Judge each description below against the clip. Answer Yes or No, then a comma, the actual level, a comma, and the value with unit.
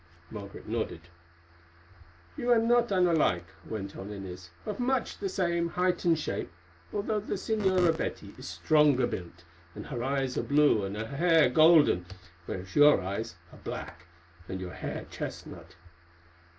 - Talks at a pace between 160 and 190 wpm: No, average, 150 wpm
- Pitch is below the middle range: No, medium, 145 Hz